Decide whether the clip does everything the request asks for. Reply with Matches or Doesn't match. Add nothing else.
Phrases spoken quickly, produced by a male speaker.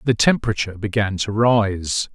Doesn't match